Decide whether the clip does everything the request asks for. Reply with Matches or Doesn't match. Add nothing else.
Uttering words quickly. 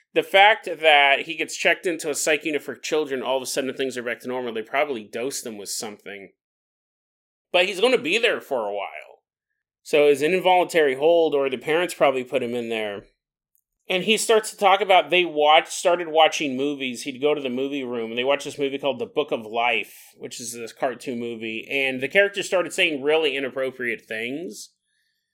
Matches